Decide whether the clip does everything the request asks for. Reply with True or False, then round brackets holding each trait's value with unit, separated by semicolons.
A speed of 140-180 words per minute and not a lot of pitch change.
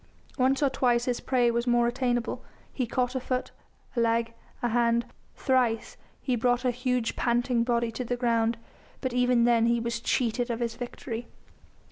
True (175 wpm; 1.2 semitones)